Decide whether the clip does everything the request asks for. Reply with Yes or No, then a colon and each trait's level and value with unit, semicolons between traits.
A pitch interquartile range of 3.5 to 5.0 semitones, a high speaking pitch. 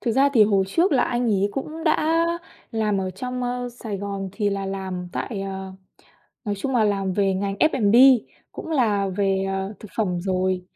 Yes: average, 4.3 semitones; high, 205 Hz